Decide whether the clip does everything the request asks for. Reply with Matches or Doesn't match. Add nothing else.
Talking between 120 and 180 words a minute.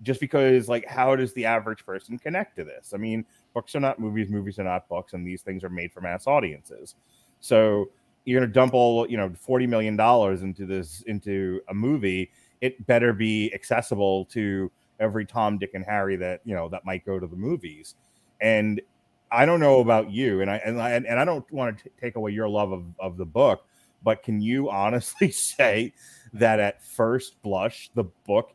Doesn't match